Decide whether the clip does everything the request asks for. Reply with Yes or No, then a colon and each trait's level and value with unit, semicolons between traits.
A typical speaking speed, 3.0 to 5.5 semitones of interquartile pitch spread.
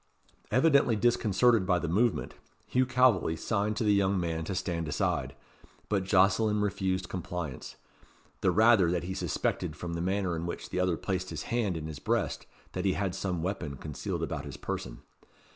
Yes: average, 175 wpm; average, 3.5 semitones